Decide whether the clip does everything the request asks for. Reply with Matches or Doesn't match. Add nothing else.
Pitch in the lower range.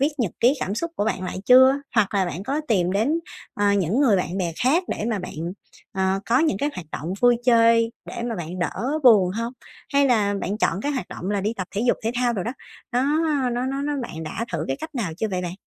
Doesn't match